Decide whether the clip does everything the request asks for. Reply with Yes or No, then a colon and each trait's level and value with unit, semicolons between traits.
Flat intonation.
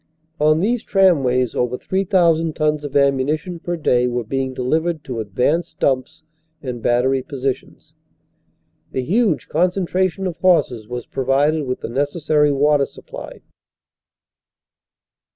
No: average, 4.7 semitones